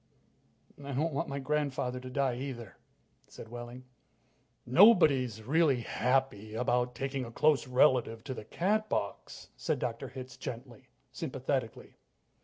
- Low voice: Yes, low, 130 Hz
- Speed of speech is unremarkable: No, slow, 125 wpm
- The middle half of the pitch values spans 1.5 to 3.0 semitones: Yes, narrow, 2.6 semitones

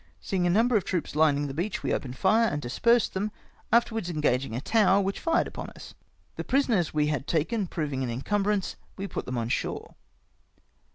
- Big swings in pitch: Yes, wide, 6.5 semitones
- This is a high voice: No, medium, 180 Hz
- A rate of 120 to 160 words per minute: No, average, 190 wpm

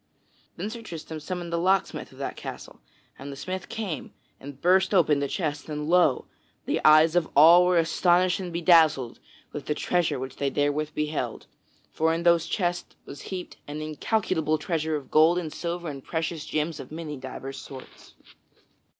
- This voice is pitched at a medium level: Yes, medium, 160 Hz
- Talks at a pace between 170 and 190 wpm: Yes, average, 175 wpm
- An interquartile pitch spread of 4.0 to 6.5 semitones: No, average, 2.9 semitones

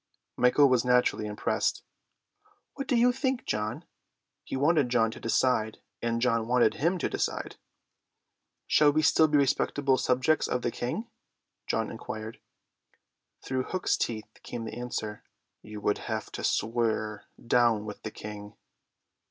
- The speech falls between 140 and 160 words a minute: Yes, average, 145 wpm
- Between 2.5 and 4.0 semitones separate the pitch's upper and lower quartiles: No, average, 4.5 semitones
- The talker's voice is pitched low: Yes, low, 120 Hz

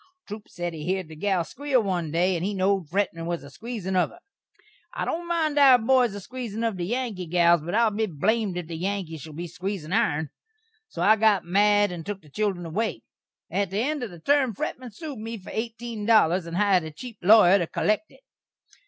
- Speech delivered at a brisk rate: Yes, fast, 225 wpm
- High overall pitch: Yes, high, 200 Hz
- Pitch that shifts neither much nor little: Yes, average, 4.5 semitones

